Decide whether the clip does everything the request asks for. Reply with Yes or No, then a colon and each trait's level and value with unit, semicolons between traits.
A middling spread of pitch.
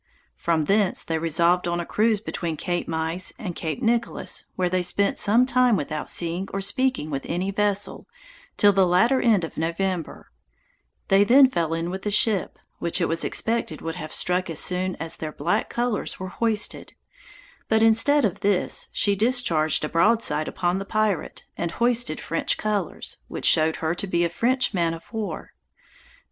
Yes: average, 4.6 semitones